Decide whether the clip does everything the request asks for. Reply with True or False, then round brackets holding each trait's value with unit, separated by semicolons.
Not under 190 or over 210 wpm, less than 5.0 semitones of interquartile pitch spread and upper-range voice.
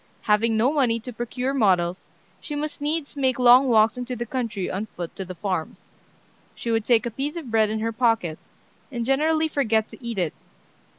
True (195 wpm; 3.6 semitones; 235 Hz)